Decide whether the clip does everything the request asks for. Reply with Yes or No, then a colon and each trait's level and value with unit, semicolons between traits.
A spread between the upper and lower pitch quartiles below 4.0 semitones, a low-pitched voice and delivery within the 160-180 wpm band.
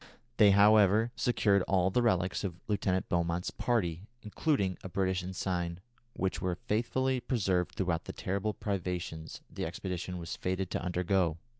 No: narrow, 2.6 semitones; very low, 95 Hz; average, 145 wpm